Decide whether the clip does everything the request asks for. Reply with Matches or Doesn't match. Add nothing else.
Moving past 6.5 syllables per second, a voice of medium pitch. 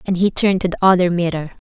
Matches